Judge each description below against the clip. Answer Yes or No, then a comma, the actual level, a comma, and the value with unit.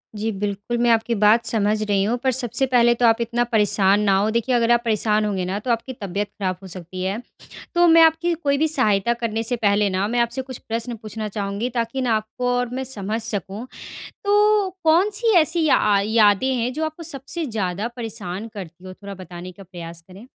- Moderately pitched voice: No, high, 225 Hz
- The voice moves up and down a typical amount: Yes, average, 3.8 semitones